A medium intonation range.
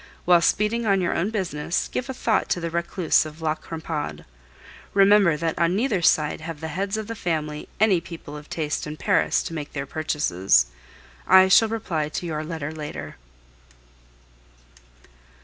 Yes: average, 4.2 semitones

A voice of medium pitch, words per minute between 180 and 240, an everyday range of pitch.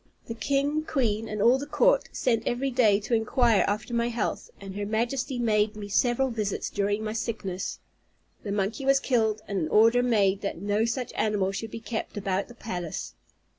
No: high, 220 Hz; average, 190 wpm; average, 3.0 semitones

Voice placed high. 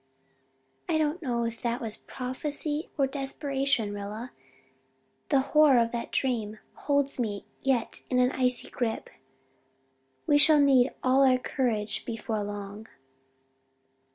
Yes: very high, 255 Hz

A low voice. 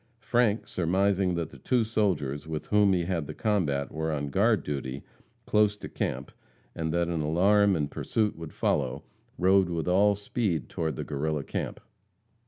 Yes: very low, 90 Hz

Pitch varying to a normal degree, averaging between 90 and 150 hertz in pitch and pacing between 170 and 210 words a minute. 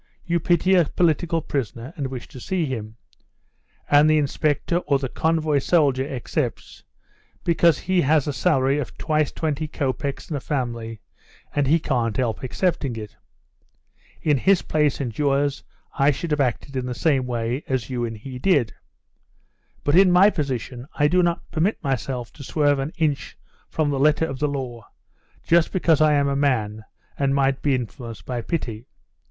Yes: average, 3.6 semitones; medium, 140 Hz; average, 175 wpm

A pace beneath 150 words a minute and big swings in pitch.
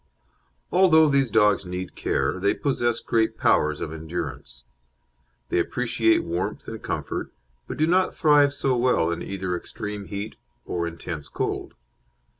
Yes: average, 140 wpm; wide, 6.8 semitones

